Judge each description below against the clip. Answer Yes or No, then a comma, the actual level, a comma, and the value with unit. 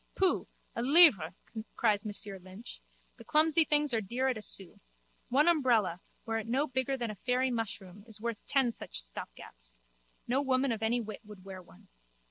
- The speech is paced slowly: No, average, 180 wpm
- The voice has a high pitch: Yes, high, 230 Hz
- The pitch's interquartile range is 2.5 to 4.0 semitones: No, average, 4.7 semitones